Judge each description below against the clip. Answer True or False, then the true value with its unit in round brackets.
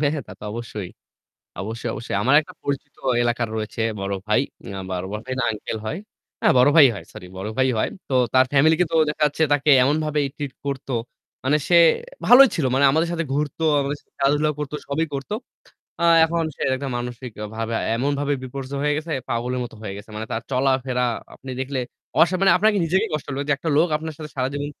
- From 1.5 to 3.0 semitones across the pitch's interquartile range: False (4.0 semitones)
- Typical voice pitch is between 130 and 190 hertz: True (135 Hz)